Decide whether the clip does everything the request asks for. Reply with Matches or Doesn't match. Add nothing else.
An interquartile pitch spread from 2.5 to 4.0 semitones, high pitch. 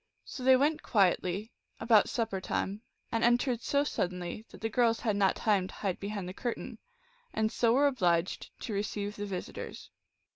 Matches